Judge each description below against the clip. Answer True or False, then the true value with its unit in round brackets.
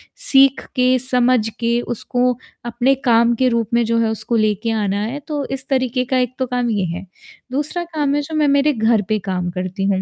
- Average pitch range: True (3.3 semitones)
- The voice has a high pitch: True (245 Hz)